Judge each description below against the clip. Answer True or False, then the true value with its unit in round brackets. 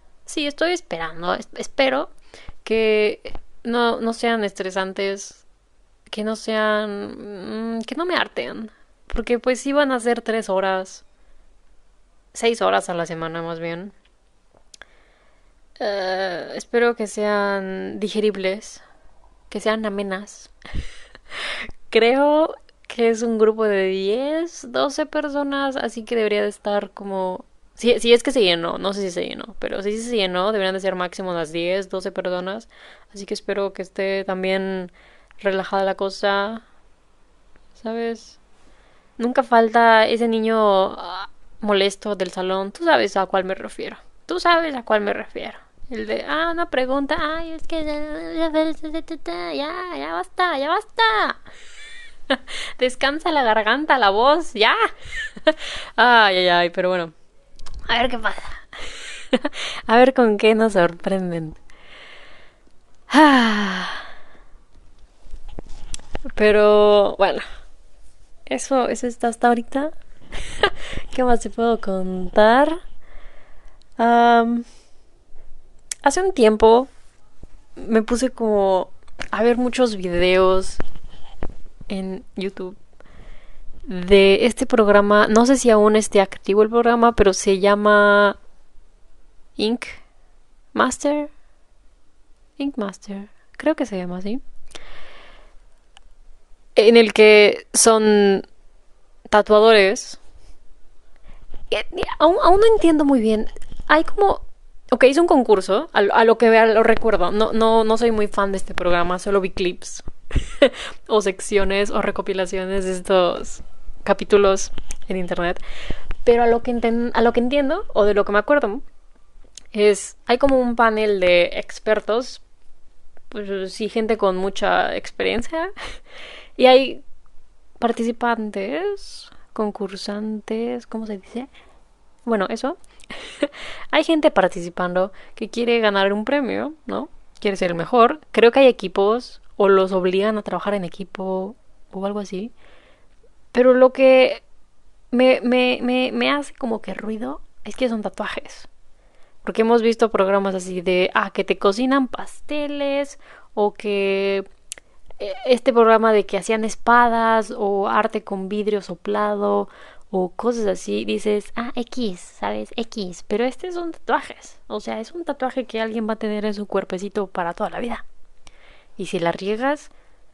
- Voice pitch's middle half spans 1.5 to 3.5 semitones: False (4.3 semitones)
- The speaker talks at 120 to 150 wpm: True (130 wpm)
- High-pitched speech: True (220 Hz)